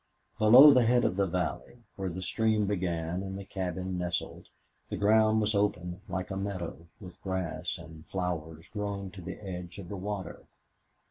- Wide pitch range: No, average, 2.7 semitones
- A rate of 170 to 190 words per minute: Yes, average, 175 wpm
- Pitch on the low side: Yes, very low, 95 Hz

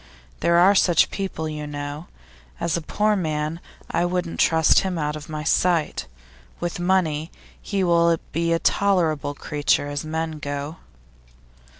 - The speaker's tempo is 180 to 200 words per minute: No, average, 150 wpm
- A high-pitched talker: No, medium, 165 Hz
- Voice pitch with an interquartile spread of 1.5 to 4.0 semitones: Yes, narrow, 2.6 semitones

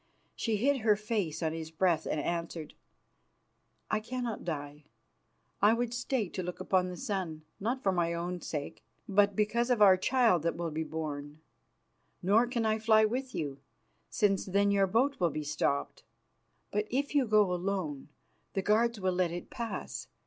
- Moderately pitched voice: No, high, 195 Hz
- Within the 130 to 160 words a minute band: No, average, 170 wpm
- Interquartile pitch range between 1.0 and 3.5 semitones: No, average, 4.9 semitones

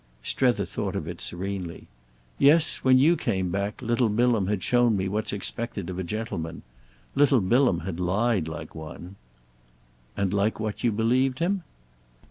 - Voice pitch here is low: Yes, low, 105 Hz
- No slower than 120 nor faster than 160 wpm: Yes, average, 155 wpm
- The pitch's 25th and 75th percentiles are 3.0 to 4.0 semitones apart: No, average, 4.6 semitones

